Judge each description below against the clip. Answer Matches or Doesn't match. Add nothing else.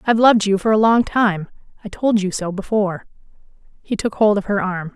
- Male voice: Doesn't match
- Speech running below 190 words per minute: Doesn't match